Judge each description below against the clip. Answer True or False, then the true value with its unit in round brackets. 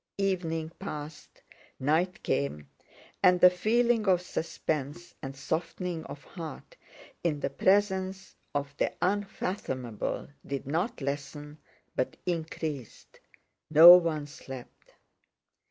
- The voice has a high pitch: False (160 Hz)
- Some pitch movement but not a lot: True (4.3 semitones)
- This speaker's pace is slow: True (105 wpm)